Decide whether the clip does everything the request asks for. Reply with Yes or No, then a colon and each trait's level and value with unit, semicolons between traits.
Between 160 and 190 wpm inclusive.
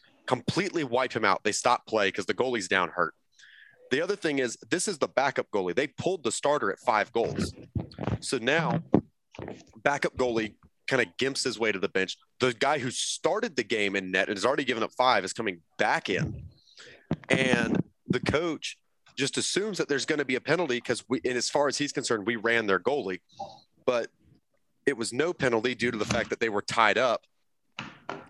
No: fast, 205 wpm